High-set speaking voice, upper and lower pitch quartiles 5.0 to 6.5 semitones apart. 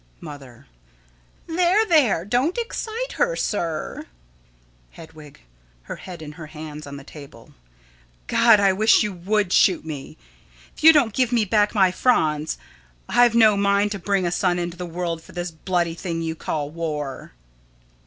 No: medium, 180 Hz; wide, 5.6 semitones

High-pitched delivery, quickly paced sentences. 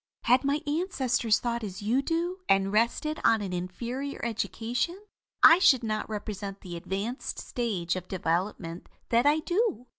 No: high, 230 Hz; average, 150 wpm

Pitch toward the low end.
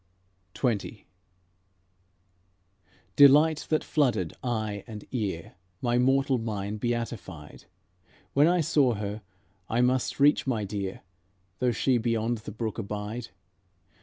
Yes: low, 115 Hz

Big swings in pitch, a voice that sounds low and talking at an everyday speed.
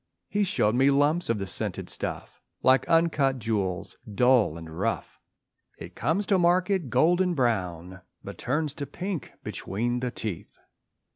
Yes: wide, 7.8 semitones; low, 130 Hz; average, 145 wpm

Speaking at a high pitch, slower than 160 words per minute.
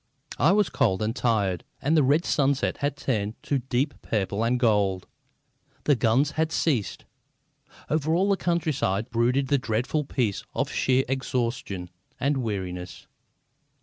No: low, 125 Hz; average, 145 wpm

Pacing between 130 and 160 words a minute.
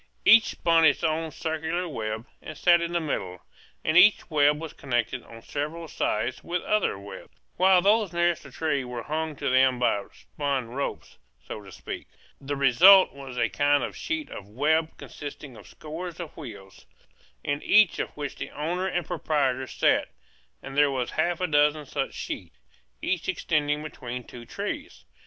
No: average, 175 wpm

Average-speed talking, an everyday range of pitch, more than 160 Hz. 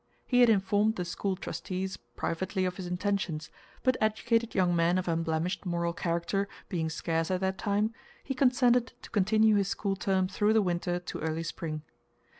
Yes: average, 175 wpm; average, 3.6 semitones; high, 190 Hz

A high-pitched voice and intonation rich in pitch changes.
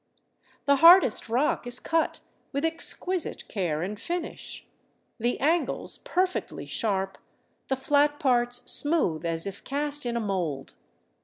Yes: very high, 255 Hz; wide, 7.0 semitones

